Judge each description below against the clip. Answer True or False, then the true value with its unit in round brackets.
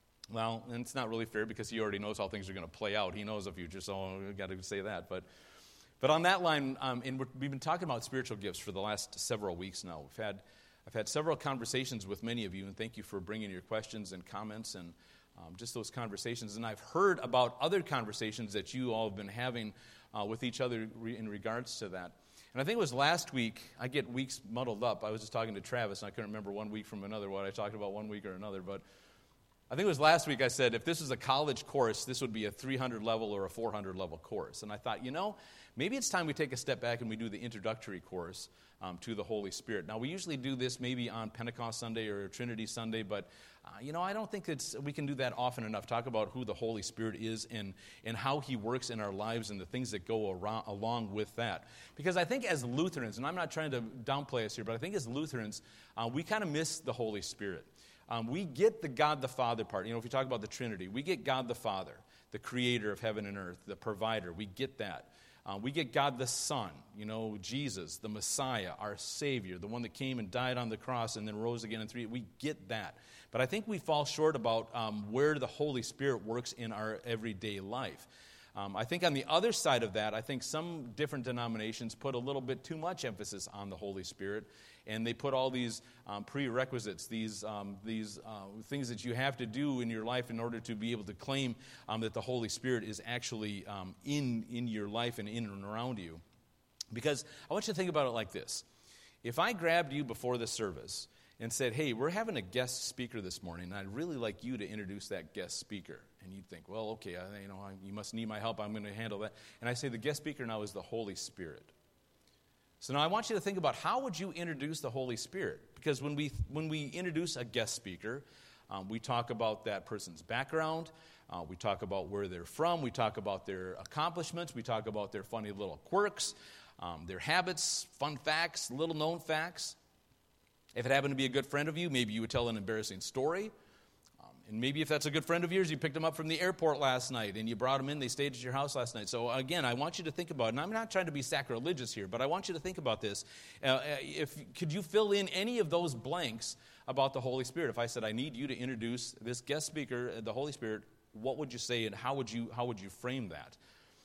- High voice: False (120 Hz)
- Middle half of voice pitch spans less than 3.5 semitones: False (4.6 semitones)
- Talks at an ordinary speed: False (250 wpm)